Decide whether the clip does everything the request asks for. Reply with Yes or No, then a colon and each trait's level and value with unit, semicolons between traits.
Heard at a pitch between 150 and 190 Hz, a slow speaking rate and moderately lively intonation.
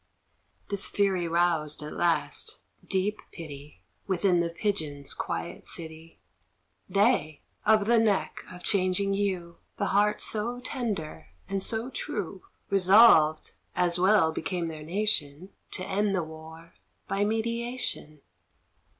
Yes: medium, 185 Hz; slow, 120 wpm; average, 4.3 semitones